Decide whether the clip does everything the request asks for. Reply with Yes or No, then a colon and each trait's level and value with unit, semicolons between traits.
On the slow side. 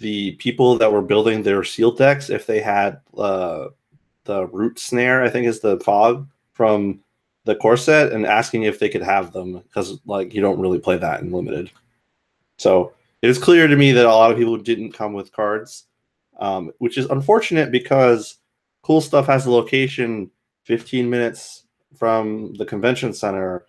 No: average, 175 wpm